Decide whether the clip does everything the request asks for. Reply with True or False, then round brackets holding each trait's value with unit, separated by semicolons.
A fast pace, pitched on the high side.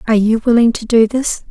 True (240 wpm; 225 Hz)